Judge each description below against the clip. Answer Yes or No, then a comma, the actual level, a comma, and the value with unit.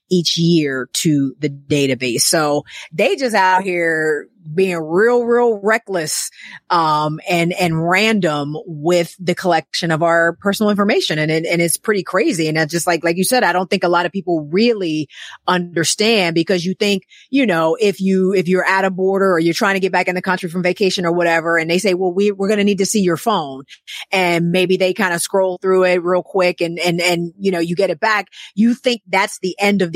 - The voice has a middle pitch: Yes, medium, 180 Hz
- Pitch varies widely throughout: No, narrow, 2.5 semitones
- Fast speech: Yes, fast, 220 wpm